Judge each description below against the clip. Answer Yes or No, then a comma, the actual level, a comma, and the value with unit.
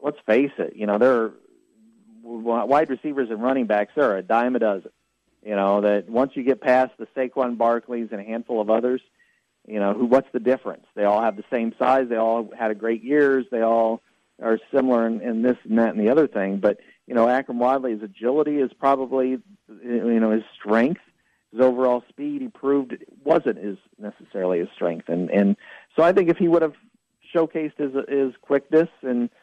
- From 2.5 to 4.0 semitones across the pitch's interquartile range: Yes, average, 3.5 semitones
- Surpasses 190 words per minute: Yes, fast, 205 wpm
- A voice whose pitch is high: No, low, 125 Hz